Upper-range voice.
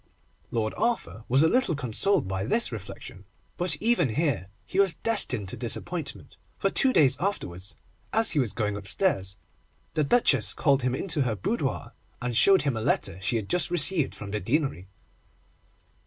No: low, 130 Hz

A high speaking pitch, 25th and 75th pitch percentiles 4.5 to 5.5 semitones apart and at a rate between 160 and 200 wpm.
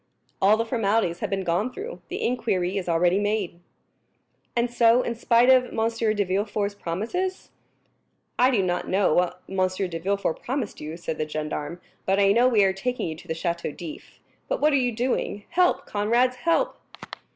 Yes: high, 205 Hz; average, 5.1 semitones; average, 185 wpm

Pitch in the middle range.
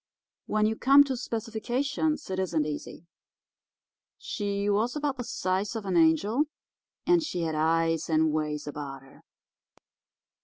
No: high, 200 Hz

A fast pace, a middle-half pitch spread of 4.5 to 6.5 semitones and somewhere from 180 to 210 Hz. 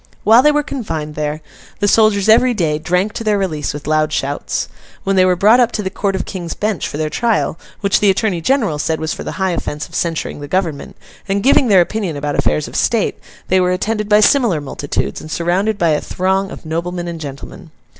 Yes: fast, 225 wpm; average, 5.1 semitones; medium, 185 Hz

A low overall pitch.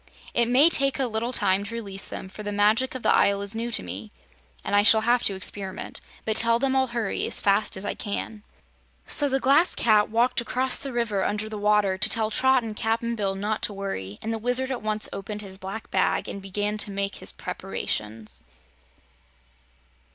No: high, 215 Hz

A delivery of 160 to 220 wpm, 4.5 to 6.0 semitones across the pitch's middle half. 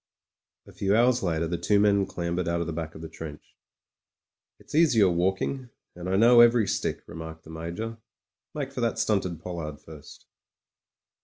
Yes: average, 170 wpm; wide, 5.6 semitones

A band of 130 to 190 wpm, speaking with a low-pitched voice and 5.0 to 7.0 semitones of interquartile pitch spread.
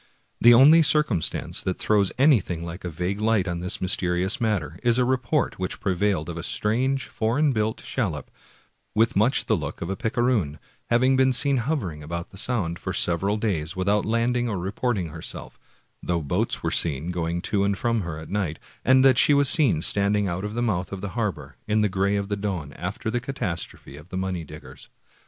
No: average, 200 wpm; low, 100 Hz; wide, 5.4 semitones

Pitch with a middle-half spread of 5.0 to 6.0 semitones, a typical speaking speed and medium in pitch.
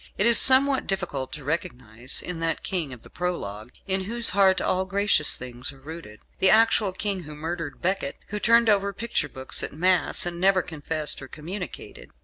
Yes: average, 5.3 semitones; average, 185 wpm; medium, 180 Hz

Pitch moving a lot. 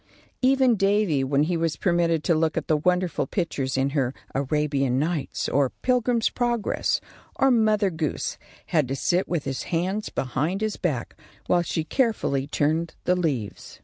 Yes: wide, 5.8 semitones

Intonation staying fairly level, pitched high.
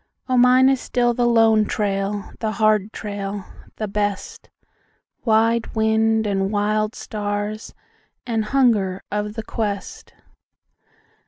Yes: narrow, 1.7 semitones; high, 215 Hz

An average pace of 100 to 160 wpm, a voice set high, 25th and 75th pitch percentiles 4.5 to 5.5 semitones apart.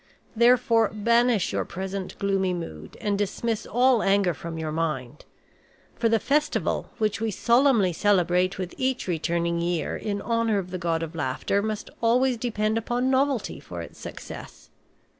Yes: average, 155 wpm; high, 205 Hz; average, 5.1 semitones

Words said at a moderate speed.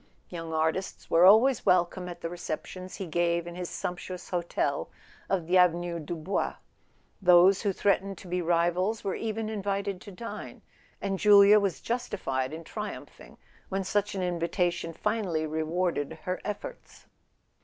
Yes: average, 155 wpm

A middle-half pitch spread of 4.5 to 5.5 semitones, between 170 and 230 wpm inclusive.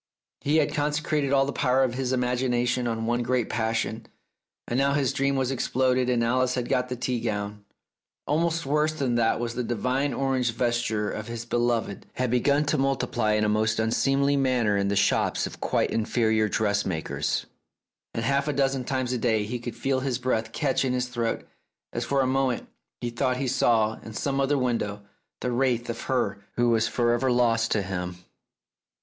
No: average, 2.8 semitones; average, 195 wpm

